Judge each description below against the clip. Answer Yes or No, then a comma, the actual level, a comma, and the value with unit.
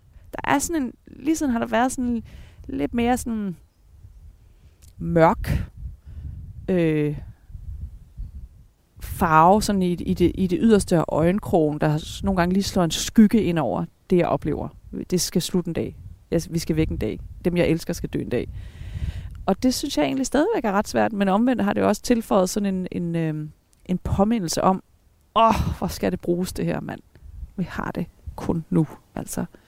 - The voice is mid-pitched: Yes, medium, 170 Hz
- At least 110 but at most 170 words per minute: No, average, 185 wpm